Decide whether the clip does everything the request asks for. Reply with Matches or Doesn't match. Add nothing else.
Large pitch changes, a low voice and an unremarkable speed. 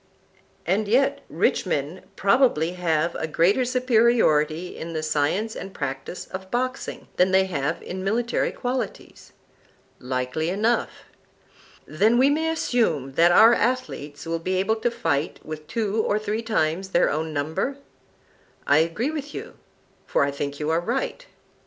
Doesn't match